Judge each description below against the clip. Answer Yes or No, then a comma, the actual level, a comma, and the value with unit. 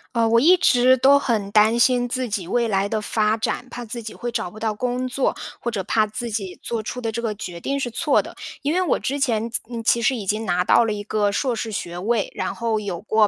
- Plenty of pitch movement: No, narrow, 2.6 semitones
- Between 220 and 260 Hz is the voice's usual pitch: Yes, high, 225 Hz